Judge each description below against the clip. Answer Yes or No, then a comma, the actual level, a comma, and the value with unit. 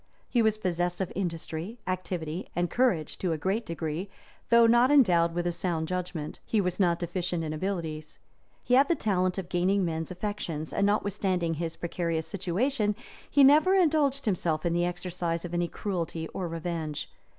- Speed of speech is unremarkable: Yes, average, 175 wpm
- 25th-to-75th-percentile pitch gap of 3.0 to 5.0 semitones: Yes, average, 3.5 semitones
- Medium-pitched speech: Yes, medium, 180 Hz